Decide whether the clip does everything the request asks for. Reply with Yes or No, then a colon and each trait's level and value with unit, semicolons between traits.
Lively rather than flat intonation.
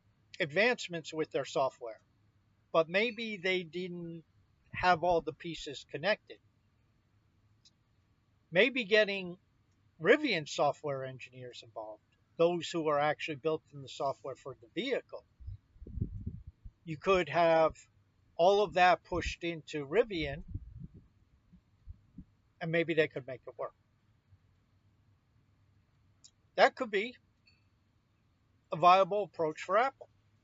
Yes: wide, 8.0 semitones